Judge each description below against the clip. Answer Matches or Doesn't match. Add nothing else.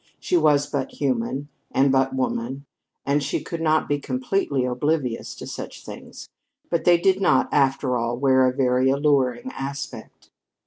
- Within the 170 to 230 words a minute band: Doesn't match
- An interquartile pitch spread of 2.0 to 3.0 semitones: Matches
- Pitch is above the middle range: Doesn't match